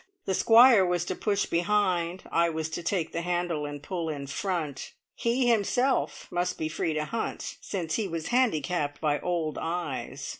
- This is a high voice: No, medium, 175 Hz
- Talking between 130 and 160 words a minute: No, average, 175 wpm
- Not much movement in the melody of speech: No, average, 4.0 semitones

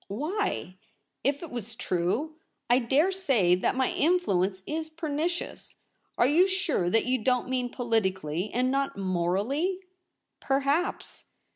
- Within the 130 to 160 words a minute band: Yes, average, 150 wpm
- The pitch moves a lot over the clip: Yes, wide, 7.8 semitones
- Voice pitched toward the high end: Yes, very high, 260 Hz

